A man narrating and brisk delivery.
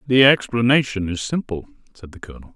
No: male; average, 165 wpm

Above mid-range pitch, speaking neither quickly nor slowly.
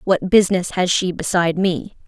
No: medium, 180 Hz; average, 175 wpm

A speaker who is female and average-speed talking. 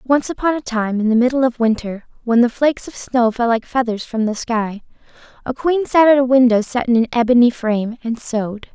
No: female; fast, 225 wpm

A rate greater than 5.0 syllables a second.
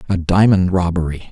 Yes: 5.4 syllables/s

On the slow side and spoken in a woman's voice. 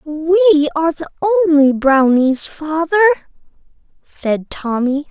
Yes: slow, 95 wpm; female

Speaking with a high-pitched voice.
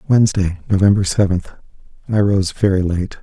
No: very low, 95 Hz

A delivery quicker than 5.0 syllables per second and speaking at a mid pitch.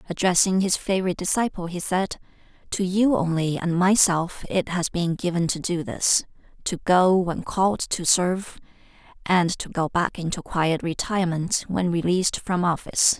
No: 4.9 syllables/s; medium, 180 Hz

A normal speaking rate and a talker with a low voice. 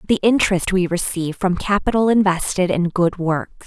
No: average, 165 wpm; medium, 185 Hz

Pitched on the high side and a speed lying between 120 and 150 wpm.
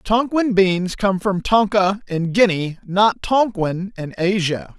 Yes: high, 195 Hz; average, 140 wpm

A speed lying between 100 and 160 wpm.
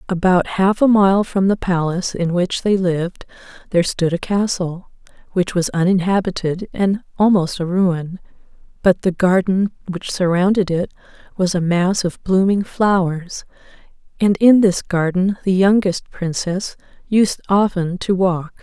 Yes: average, 145 wpm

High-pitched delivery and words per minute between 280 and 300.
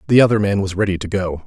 No: low, 100 Hz; fast, 285 wpm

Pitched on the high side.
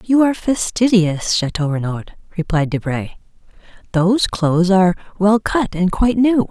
Yes: high, 195 Hz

